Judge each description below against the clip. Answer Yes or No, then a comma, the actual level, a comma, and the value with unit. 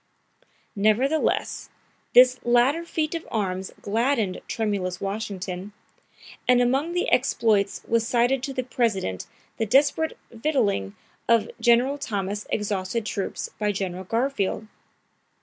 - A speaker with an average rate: No, slow, 115 wpm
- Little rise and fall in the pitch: No, average, 4.5 semitones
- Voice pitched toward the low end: No, high, 225 Hz